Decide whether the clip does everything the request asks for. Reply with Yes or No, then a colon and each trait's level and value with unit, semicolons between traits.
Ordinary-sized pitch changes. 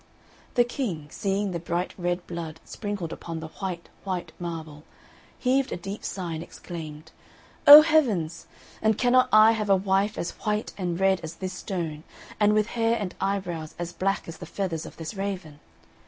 Yes: average, 3.9 semitones